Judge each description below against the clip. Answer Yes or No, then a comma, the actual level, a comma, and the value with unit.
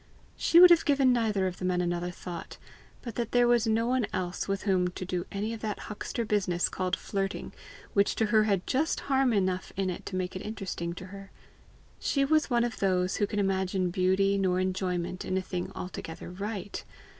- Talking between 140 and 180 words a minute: No, fast, 205 wpm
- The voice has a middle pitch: No, high, 195 Hz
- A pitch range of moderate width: Yes, average, 3.4 semitones